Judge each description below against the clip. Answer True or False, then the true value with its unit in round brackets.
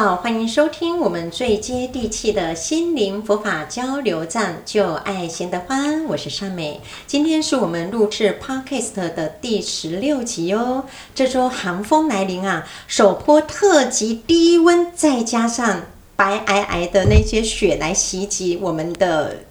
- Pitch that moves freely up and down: True (6.3 semitones)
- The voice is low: False (215 Hz)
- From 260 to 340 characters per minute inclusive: False (235 characters per minute)